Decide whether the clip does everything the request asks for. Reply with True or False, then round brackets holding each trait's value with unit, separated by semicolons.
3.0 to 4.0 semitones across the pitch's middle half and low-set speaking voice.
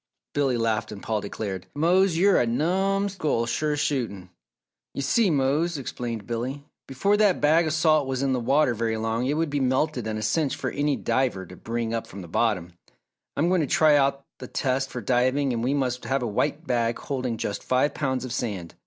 False (4.6 semitones; 130 Hz)